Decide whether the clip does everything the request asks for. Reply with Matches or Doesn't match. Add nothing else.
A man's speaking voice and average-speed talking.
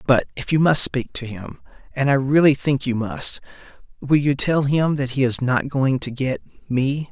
Matches